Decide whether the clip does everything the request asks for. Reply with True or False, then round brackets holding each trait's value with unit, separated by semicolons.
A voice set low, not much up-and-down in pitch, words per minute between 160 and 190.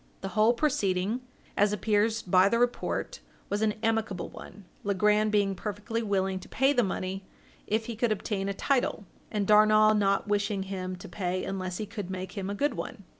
False (205 Hz; 2.2 semitones; 185 wpm)